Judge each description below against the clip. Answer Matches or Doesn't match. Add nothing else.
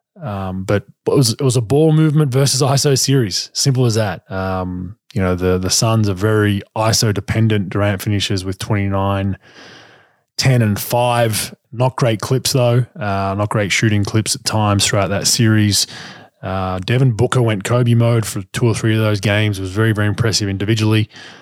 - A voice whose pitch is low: Matches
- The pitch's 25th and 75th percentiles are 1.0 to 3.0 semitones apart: Doesn't match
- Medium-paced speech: Matches